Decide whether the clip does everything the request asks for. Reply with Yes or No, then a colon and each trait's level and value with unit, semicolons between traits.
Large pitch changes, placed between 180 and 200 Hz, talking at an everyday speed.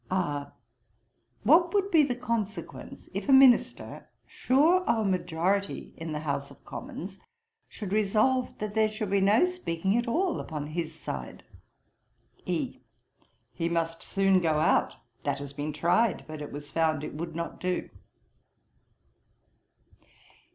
Yes: wide, 6.5 semitones; high, 190 Hz; average, 145 wpm